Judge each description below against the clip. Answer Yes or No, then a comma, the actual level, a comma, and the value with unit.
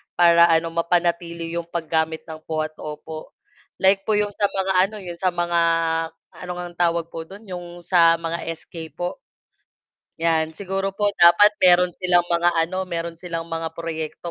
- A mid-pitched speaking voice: Yes, medium, 170 Hz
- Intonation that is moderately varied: No, narrow, 1.5 semitones